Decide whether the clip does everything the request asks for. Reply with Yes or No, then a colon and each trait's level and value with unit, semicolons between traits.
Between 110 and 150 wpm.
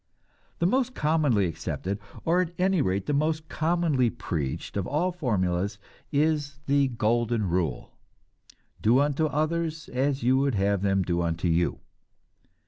Yes: average, 140 wpm